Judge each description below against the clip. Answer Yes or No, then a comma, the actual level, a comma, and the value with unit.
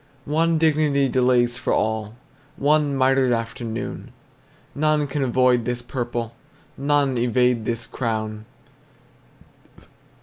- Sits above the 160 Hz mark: No, low, 125 Hz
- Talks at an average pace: No, slow, 100 wpm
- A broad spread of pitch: No, average, 3.3 semitones